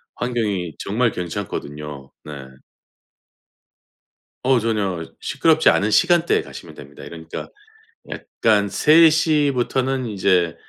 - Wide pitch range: Yes, wide, 7.6 semitones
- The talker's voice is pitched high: No, low, 105 Hz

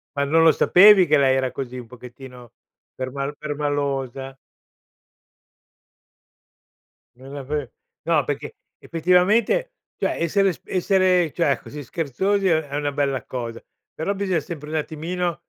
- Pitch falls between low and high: Yes, medium, 150 Hz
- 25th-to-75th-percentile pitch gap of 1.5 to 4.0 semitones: No, average, 4.7 semitones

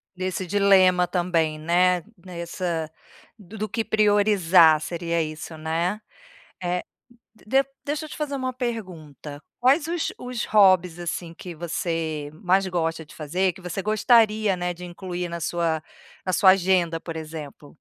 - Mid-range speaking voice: Yes, medium, 180 Hz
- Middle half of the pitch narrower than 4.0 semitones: Yes, average, 3.6 semitones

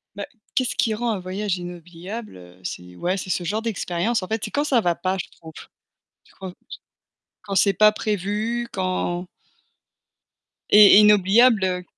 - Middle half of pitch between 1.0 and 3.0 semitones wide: No, average, 3.4 semitones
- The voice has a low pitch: No, high, 195 Hz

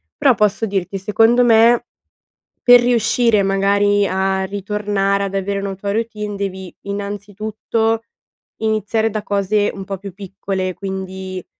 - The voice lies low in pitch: No, high, 200 Hz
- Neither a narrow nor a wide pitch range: No, narrow, 2.0 semitones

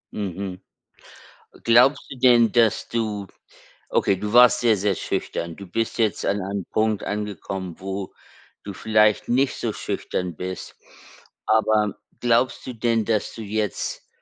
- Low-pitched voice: Yes, low, 105 Hz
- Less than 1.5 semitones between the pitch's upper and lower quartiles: No, average, 2.8 semitones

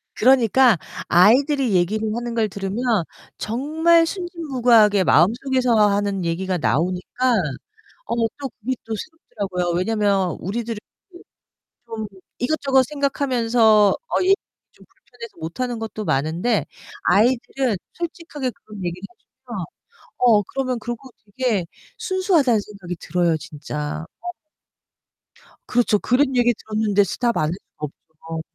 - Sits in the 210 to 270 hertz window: Yes, high, 230 Hz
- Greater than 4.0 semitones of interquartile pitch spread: Yes, average, 5.1 semitones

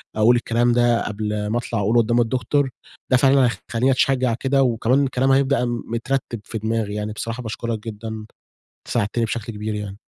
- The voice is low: Yes, low, 115 Hz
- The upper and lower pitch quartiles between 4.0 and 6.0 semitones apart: No, narrow, 2.6 semitones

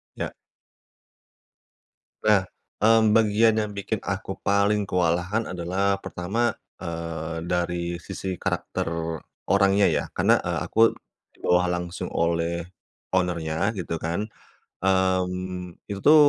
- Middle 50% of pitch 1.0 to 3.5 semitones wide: Yes, average, 2.8 semitones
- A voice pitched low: Yes, very low, 90 Hz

